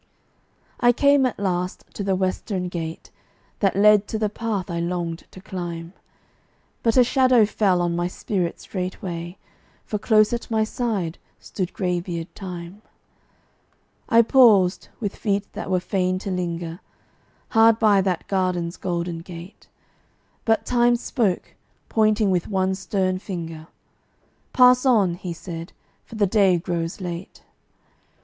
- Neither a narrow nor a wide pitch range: Yes, average, 3.6 semitones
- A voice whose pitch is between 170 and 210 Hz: Yes, high, 190 Hz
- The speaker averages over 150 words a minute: No, average, 140 wpm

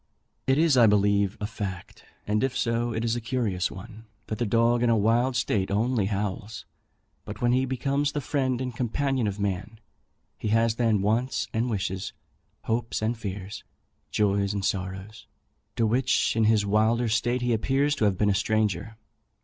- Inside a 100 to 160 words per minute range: No, average, 180 wpm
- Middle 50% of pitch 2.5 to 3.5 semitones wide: Yes, average, 2.9 semitones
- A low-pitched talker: Yes, low, 110 Hz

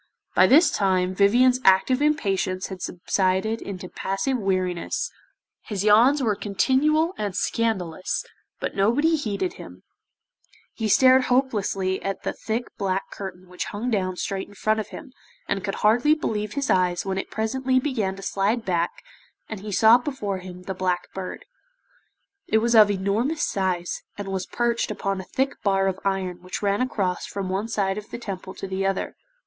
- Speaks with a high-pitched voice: Yes, high, 200 Hz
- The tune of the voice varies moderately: Yes, average, 3.9 semitones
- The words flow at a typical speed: Yes, average, 170 wpm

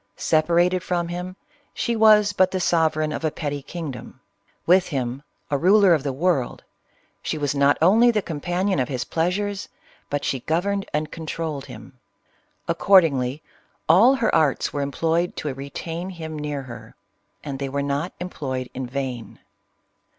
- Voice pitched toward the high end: No, medium, 155 Hz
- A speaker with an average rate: Yes, average, 165 wpm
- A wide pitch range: No, average, 4.6 semitones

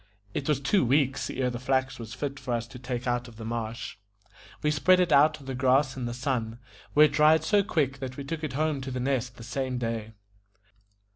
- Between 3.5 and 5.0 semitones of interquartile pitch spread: No, average, 3.0 semitones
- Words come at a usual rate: No, fast, 230 wpm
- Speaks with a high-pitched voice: No, low, 130 Hz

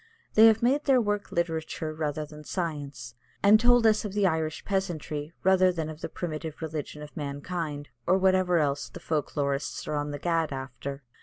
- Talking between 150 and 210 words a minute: Yes, average, 185 wpm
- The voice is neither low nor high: Yes, medium, 160 Hz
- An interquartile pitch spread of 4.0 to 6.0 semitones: Yes, average, 4.3 semitones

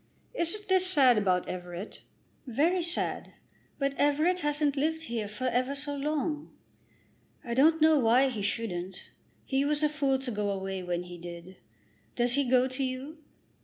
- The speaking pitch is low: No, very high, 265 Hz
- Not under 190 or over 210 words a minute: No, average, 165 wpm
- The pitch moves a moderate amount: No, wide, 6.2 semitones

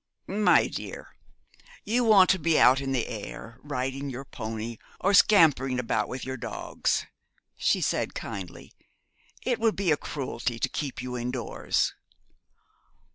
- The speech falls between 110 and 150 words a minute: Yes, average, 140 wpm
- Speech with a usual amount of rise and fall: No, wide, 6.0 semitones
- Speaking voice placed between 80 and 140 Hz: Yes, low, 135 Hz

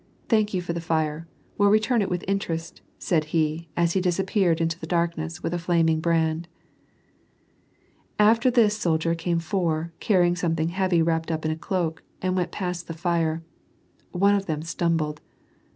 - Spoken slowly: No, average, 170 wpm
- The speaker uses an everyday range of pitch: No, narrow, 2.3 semitones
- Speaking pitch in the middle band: Yes, medium, 170 Hz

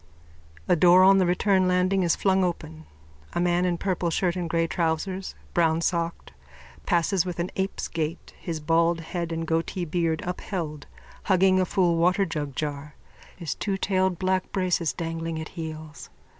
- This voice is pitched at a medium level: Yes, medium, 175 Hz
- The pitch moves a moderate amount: No, narrow, 2.1 semitones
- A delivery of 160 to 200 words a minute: No, average, 150 wpm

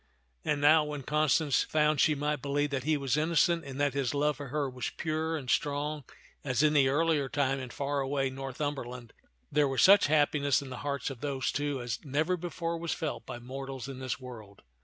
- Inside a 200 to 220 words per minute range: Yes, fast, 205 wpm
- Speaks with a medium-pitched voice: Yes, medium, 145 Hz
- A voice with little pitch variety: Yes, narrow, 2.2 semitones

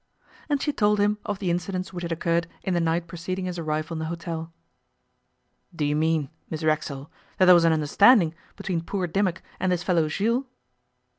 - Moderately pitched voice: Yes, medium, 170 Hz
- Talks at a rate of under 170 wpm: No, average, 195 wpm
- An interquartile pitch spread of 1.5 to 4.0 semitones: Yes, average, 2.7 semitones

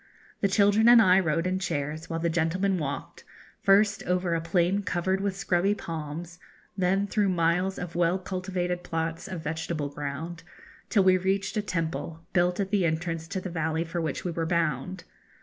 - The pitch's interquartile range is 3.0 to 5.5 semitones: No, narrow, 2.6 semitones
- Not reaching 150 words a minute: No, average, 180 wpm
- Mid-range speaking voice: Yes, medium, 175 Hz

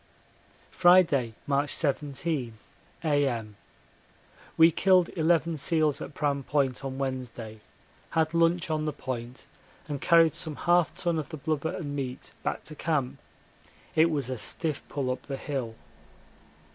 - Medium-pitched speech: Yes, medium, 145 Hz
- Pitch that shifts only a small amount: No, average, 3.7 semitones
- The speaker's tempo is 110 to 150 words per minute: Yes, average, 140 wpm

